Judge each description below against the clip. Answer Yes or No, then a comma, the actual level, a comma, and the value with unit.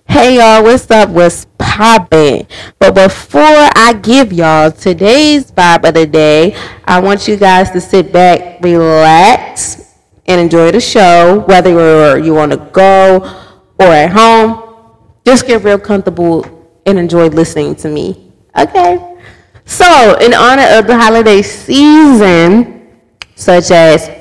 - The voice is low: No, high, 190 Hz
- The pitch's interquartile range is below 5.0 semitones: No, average, 5.3 semitones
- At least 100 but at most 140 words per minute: Yes, slow, 135 wpm